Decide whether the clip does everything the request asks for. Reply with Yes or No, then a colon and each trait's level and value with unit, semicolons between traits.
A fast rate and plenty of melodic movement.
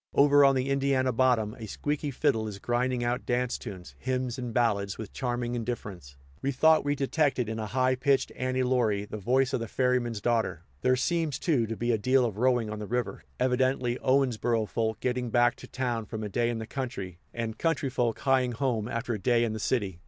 No: fast, 210 wpm; average, 2.7 semitones